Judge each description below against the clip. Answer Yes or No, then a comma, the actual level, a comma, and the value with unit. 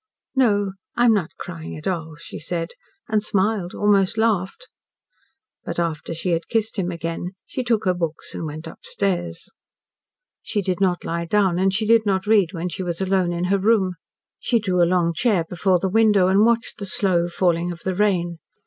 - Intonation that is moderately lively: Yes, average, 3.2 semitones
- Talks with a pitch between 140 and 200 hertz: Yes, medium, 185 Hz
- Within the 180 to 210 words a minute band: Yes, average, 195 wpm